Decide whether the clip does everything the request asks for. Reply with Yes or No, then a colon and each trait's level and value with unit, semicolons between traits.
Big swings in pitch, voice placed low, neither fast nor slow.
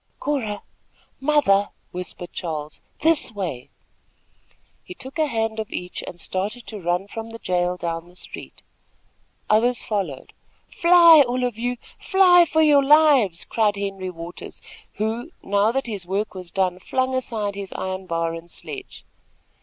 No: wide, 6.2 semitones; high, 210 Hz; average, 150 wpm